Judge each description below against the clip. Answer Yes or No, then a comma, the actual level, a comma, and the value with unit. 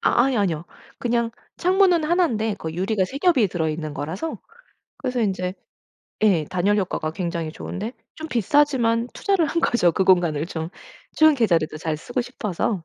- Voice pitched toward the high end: Yes, high, 210 Hz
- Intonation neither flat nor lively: No, wide, 7.2 semitones